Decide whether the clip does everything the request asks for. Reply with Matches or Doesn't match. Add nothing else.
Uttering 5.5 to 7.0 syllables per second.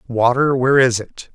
Doesn't match